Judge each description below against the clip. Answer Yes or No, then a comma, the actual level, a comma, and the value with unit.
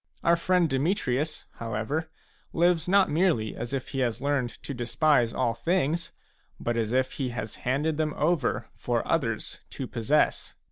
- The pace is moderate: Yes, average, 155 wpm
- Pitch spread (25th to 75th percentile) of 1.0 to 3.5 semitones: No, average, 5.1 semitones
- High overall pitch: No, medium, 140 Hz